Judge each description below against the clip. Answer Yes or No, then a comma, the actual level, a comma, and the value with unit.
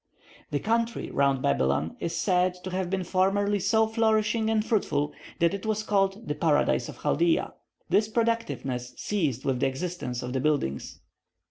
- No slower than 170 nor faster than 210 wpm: No, average, 160 wpm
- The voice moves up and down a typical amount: No, wide, 7.4 semitones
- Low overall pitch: No, medium, 185 Hz